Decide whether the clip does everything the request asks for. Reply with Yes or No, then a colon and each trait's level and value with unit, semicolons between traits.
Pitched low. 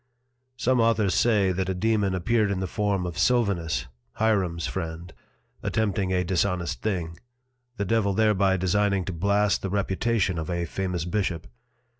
Yes: very low, 95 Hz